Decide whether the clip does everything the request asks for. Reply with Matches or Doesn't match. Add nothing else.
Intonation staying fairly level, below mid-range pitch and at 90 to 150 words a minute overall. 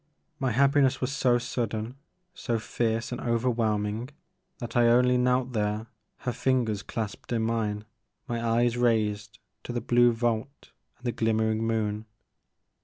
Matches